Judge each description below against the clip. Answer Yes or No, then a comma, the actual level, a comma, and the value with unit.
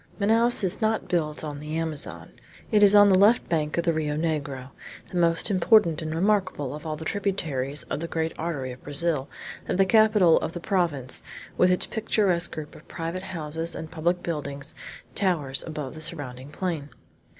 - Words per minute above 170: Yes, average, 185 wpm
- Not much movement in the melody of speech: No, average, 3.8 semitones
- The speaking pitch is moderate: Yes, medium, 165 Hz